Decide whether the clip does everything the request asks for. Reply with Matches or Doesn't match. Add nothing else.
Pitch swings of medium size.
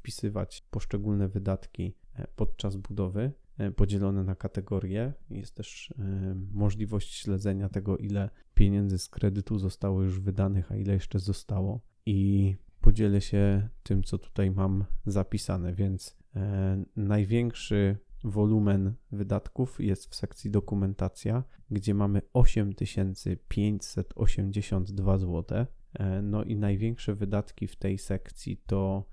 Doesn't match